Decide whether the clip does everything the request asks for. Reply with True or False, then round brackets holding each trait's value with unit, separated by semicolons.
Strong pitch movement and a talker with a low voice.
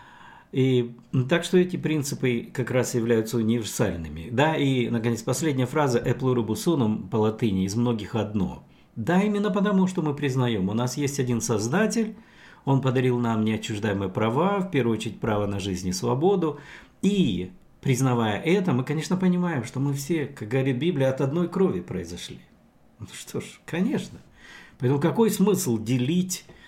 True (6.5 semitones; 130 Hz)